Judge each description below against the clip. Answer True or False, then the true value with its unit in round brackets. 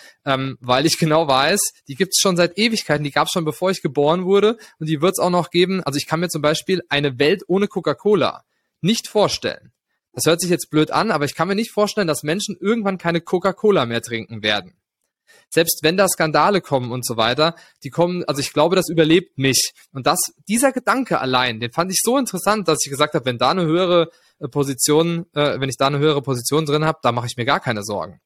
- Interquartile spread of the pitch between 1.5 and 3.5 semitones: False (4.7 semitones)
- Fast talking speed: True (230 wpm)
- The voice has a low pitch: False (160 Hz)